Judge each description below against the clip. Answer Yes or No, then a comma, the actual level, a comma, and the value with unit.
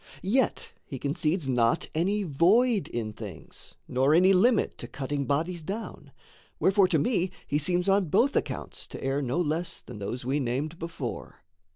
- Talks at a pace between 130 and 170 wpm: Yes, average, 165 wpm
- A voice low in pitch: No, medium, 160 Hz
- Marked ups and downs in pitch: Yes, wide, 5.7 semitones